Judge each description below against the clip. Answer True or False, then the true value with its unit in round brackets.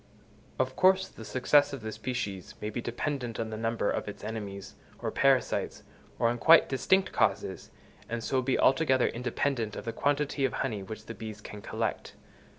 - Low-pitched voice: True (120 Hz)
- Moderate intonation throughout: True (3.7 semitones)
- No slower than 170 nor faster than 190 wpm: True (180 wpm)